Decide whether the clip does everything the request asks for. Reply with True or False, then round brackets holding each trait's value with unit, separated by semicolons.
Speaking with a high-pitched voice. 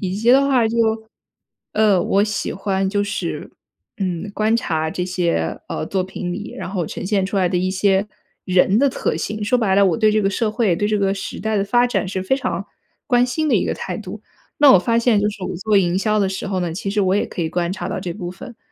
True (200 Hz)